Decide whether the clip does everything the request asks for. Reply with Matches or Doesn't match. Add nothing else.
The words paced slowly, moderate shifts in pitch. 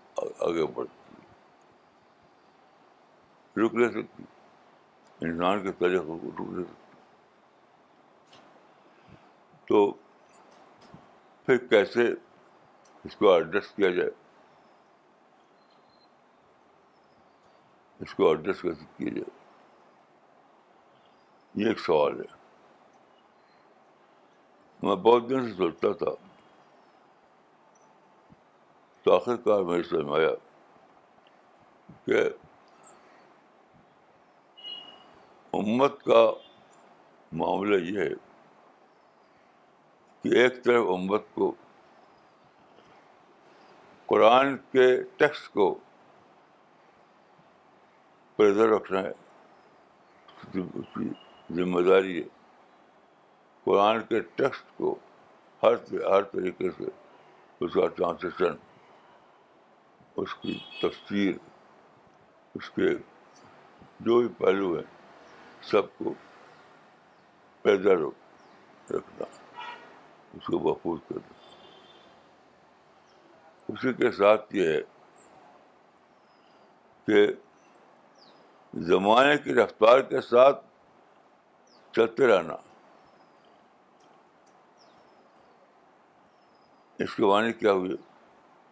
Matches